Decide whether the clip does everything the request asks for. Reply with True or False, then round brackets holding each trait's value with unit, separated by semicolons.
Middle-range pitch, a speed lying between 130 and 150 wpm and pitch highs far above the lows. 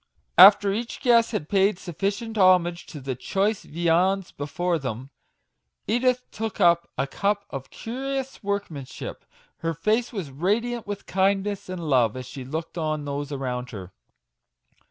True (180 Hz; 145 wpm; 6.3 semitones)